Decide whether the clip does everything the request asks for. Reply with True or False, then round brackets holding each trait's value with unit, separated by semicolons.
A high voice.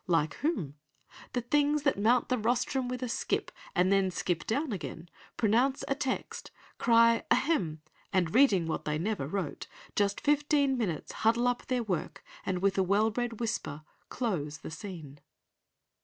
True (220 Hz)